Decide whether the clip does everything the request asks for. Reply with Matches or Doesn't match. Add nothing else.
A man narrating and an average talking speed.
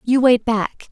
Doesn't match